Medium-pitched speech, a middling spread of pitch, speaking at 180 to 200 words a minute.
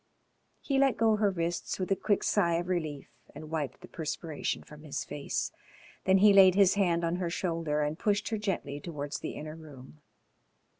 Yes: medium, 170 Hz; average, 4.2 semitones; average, 190 wpm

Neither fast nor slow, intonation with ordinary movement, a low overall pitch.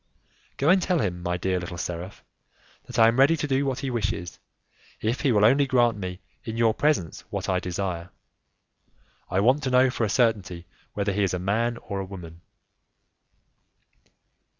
No: average, 180 wpm; wide, 5.7 semitones; low, 105 Hz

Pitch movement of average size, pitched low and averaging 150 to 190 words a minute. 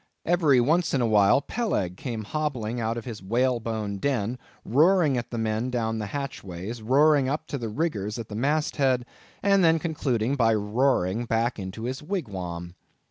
Yes: average, 4.7 semitones; low, 120 Hz; average, 175 wpm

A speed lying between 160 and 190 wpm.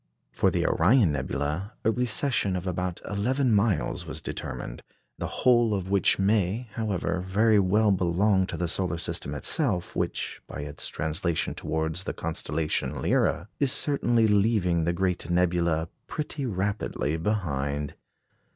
No: average, 140 wpm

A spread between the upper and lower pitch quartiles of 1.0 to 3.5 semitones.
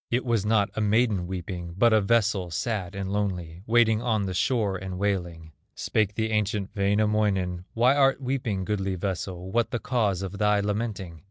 Yes: average, 2.9 semitones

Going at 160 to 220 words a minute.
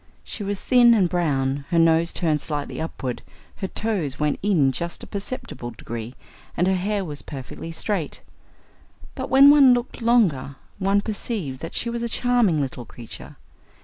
Yes: average, 165 wpm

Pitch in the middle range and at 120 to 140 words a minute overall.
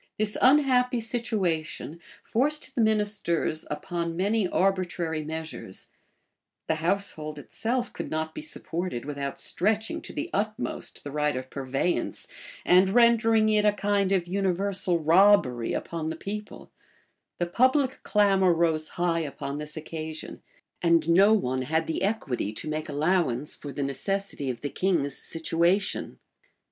Yes: medium, 175 Hz; slow, 135 wpm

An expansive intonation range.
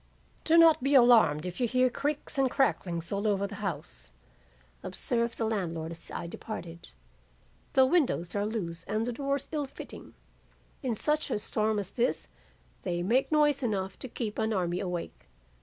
Yes: wide, 6.5 semitones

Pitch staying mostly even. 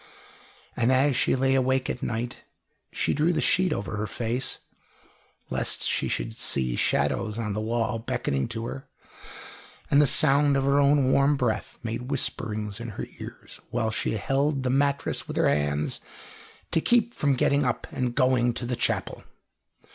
No: average, 3.6 semitones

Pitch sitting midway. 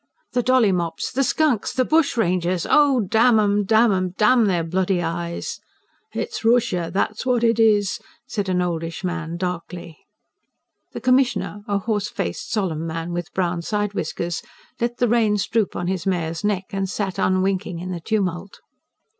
No: high, 195 Hz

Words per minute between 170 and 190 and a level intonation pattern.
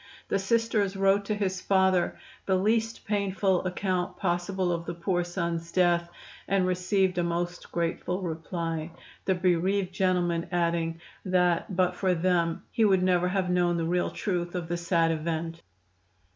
No: average, 155 wpm; narrow, 1.9 semitones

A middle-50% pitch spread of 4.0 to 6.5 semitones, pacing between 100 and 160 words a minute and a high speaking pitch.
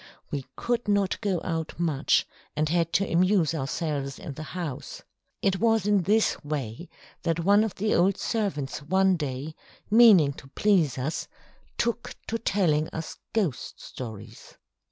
No: wide, 5.5 semitones; average, 150 wpm; medium, 170 Hz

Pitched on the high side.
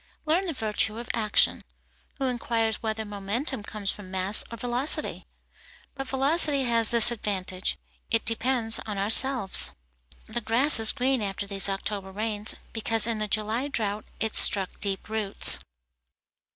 Yes: high, 220 Hz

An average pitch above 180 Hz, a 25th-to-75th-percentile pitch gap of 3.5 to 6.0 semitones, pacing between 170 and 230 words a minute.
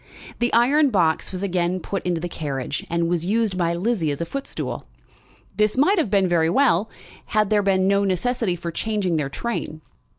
Yes: high, 190 Hz; average, 4.6 semitones; average, 190 wpm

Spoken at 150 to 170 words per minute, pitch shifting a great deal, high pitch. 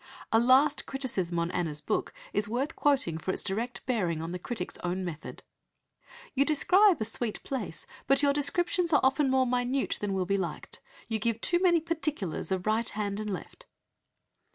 No: average, 180 wpm; wide, 6.9 semitones; high, 230 Hz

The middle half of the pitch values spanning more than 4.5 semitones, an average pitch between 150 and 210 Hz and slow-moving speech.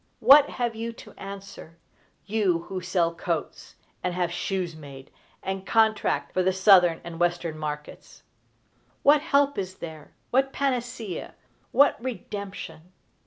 Yes: average, 5.0 semitones; high, 190 Hz; slow, 130 wpm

